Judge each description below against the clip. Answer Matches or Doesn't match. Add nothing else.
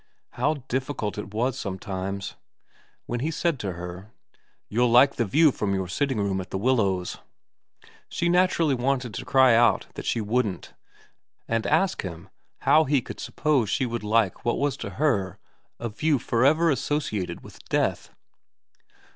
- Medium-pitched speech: Doesn't match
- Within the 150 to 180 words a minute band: Matches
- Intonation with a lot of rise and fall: Matches